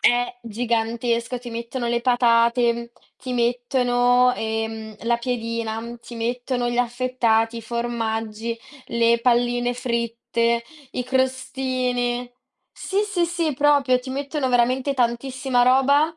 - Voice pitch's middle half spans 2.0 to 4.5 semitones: No, narrow, 1.5 semitones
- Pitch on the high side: Yes, high, 245 Hz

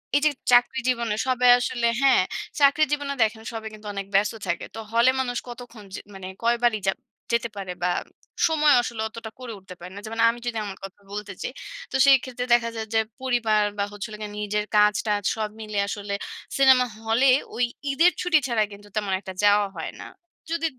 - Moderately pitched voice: No, high, 225 Hz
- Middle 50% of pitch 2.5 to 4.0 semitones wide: Yes, average, 3.3 semitones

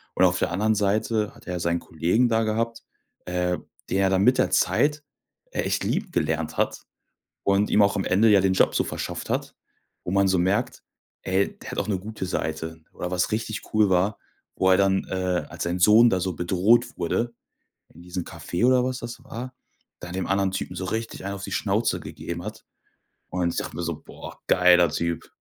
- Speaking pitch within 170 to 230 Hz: No, very low, 95 Hz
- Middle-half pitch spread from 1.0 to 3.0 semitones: No, average, 3.4 semitones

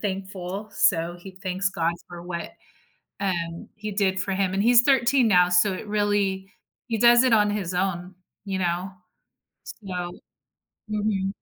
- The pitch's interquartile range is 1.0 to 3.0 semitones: Yes, narrow, 2.6 semitones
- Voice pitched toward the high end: Yes, high, 195 Hz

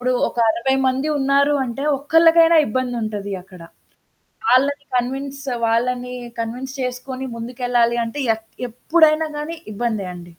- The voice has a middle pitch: No, very high, 255 Hz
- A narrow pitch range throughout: No, average, 3.2 semitones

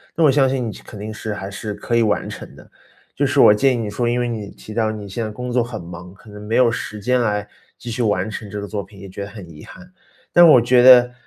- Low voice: Yes, low, 110 Hz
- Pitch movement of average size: Yes, average, 3.2 semitones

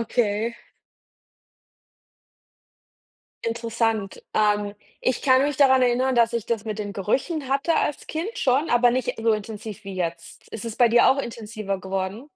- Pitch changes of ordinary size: Yes, average, 3.7 semitones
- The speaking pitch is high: Yes, high, 230 Hz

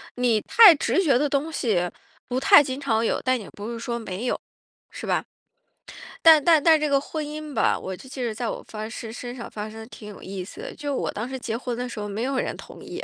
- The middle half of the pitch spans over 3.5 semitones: Yes, average, 4.5 semitones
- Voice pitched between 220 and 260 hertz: Yes, high, 245 Hz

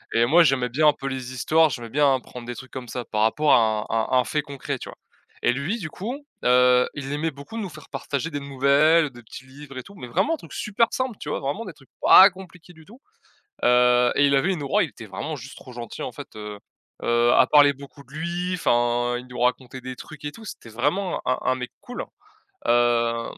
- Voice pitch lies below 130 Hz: No, low, 135 Hz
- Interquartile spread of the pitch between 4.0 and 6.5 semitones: Yes, average, 4.4 semitones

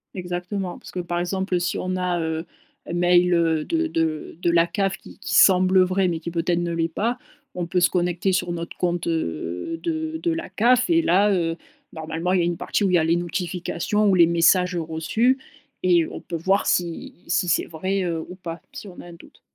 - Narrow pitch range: Yes, narrow, 2.0 semitones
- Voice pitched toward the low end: No, medium, 175 Hz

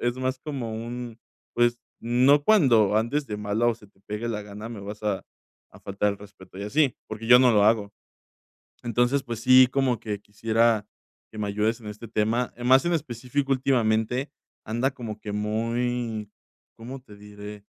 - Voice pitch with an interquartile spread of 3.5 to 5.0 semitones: No, average, 3.0 semitones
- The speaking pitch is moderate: No, low, 115 Hz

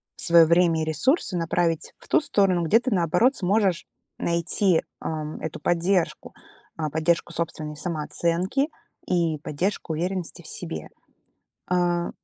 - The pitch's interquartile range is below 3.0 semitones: Yes, narrow, 2.4 semitones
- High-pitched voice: No, medium, 170 Hz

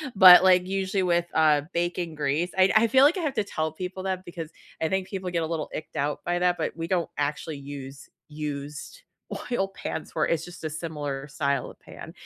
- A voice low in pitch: No, medium, 170 Hz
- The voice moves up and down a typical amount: Yes, average, 3.8 semitones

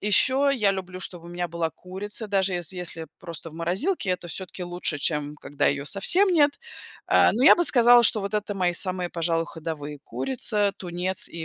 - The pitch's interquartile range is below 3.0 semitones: No, average, 3.7 semitones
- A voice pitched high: No, medium, 180 Hz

